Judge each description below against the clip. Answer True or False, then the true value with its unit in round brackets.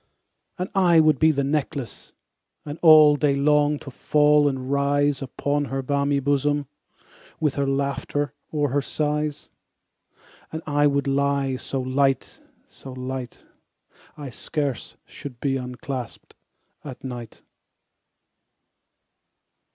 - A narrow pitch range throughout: True (1.6 semitones)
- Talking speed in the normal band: False (120 wpm)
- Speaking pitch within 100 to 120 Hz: False (140 Hz)